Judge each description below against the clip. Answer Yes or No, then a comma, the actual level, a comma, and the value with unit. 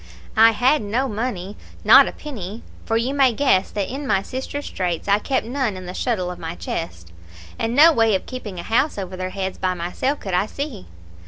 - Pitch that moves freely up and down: Yes, wide, 5.7 semitones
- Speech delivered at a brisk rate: Yes, fast, 215 wpm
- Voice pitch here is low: No, high, 215 Hz